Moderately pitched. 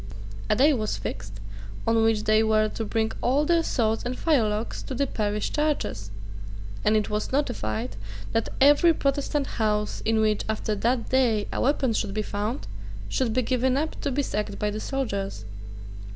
No: high, 225 Hz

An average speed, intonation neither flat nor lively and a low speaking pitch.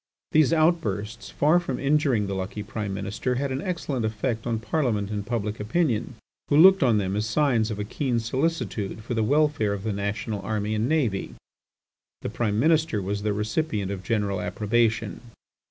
Yes: average, 175 wpm; average, 4.9 semitones; low, 110 Hz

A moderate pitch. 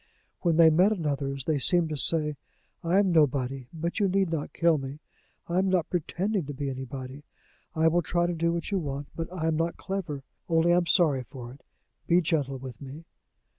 Yes: medium, 160 Hz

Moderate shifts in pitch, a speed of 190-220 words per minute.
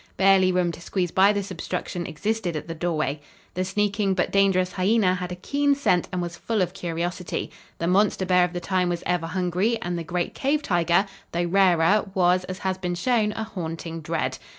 No: narrow, 2.2 semitones; average, 200 wpm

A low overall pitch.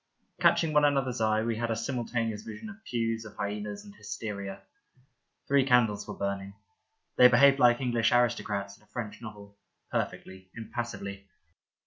Yes: low, 115 Hz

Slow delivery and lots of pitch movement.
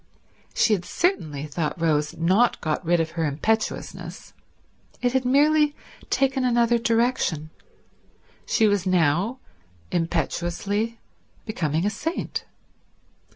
Yes: slow, 110 wpm; wide, 6.8 semitones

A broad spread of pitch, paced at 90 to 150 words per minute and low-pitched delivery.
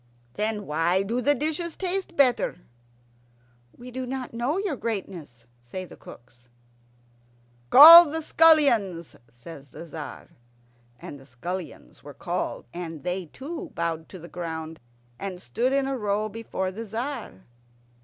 No: wide, 8.3 semitones; average, 140 wpm; high, 205 Hz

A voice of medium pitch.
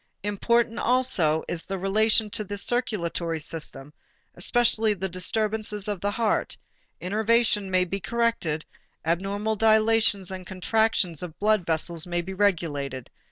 No: high, 200 Hz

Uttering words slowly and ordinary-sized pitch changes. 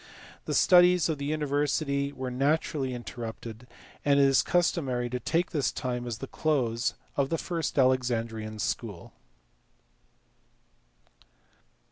Yes: slow, 120 wpm; average, 3.8 semitones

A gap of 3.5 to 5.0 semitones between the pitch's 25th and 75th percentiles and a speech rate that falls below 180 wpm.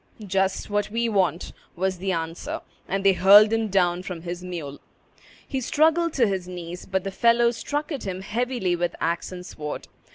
No: average, 4.2 semitones; average, 185 wpm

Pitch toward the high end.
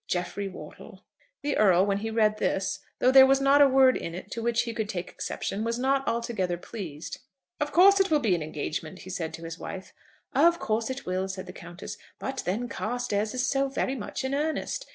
Yes: high, 225 Hz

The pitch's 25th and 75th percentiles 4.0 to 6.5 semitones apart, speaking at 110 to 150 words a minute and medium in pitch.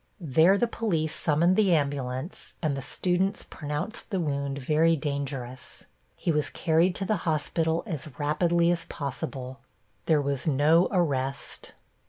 No: average, 3.6 semitones; average, 140 wpm; medium, 155 Hz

